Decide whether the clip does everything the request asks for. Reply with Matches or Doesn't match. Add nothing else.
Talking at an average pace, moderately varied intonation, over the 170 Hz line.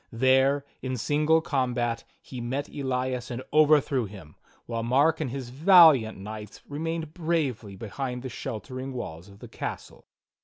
Doesn't match